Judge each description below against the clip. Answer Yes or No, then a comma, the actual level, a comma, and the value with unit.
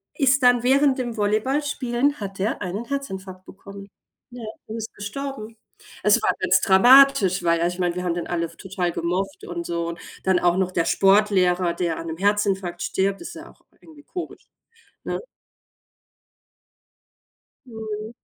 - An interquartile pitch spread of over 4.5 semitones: Yes, average, 5.2 semitones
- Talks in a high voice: Yes, high, 200 Hz